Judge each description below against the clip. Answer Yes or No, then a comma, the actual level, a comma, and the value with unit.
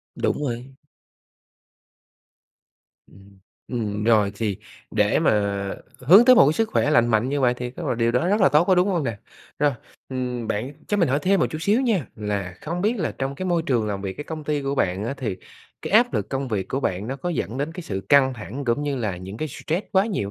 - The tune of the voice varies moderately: No, wide, 6.9 semitones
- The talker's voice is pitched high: No, low, 135 Hz